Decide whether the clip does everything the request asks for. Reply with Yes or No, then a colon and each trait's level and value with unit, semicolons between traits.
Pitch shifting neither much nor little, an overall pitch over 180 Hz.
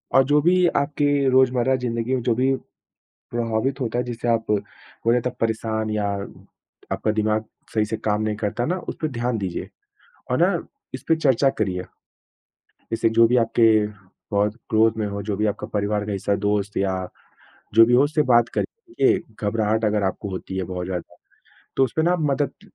No: average, 3.7 semitones; low, 115 Hz